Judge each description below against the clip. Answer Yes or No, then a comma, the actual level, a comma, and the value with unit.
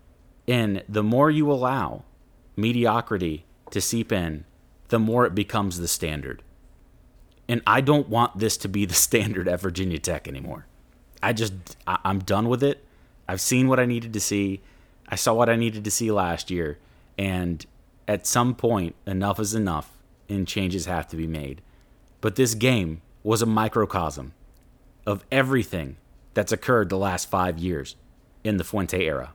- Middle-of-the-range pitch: No, low, 100 Hz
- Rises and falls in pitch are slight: No, average, 4.6 semitones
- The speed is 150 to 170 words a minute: Yes, average, 165 wpm